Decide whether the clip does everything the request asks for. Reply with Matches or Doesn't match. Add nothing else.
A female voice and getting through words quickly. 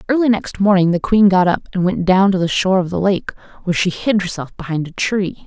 Matches